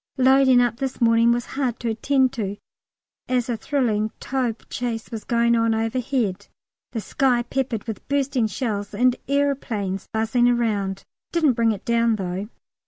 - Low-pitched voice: No, high, 235 Hz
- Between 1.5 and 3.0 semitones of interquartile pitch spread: Yes, average, 2.7 semitones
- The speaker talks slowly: No, average, 155 wpm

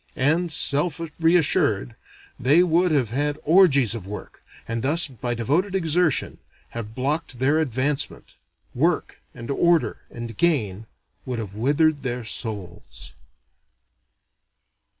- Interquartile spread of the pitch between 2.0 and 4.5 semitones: No, wide, 5.6 semitones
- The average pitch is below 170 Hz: Yes, medium, 140 Hz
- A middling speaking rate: No, slow, 120 wpm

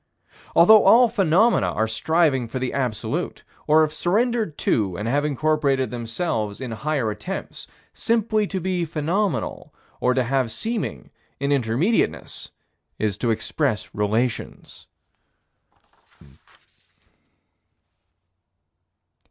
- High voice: No, medium, 140 Hz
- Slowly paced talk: Yes, slow, 105 wpm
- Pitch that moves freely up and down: Yes, wide, 7.9 semitones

